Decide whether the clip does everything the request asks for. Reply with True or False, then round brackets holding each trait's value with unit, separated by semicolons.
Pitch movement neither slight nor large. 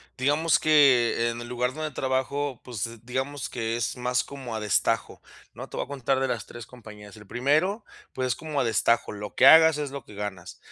True (3.5 semitones)